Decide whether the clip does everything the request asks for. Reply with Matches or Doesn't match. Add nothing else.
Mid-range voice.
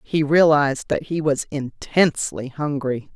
Matches